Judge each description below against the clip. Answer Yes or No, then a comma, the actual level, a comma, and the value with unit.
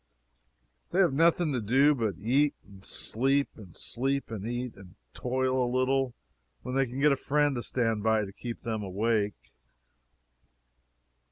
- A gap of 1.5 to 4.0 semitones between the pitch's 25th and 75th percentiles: Yes, average, 3.6 semitones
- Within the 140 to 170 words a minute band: Yes, average, 160 wpm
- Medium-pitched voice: No, low, 125 Hz